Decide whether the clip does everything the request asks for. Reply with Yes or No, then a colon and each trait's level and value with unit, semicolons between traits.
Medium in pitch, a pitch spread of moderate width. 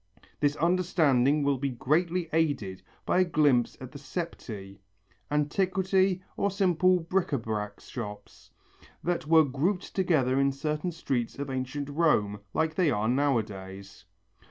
No: medium, 145 Hz; wide, 5.8 semitones